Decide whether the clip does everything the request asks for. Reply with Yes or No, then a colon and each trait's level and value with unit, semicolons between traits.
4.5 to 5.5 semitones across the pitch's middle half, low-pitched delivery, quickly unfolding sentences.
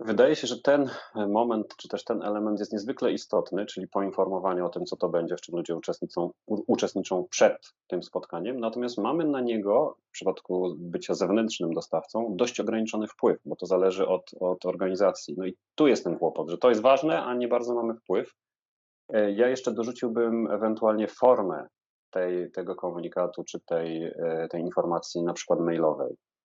Yes: average, 4.8 semitones; low, 105 Hz; fast, 170 wpm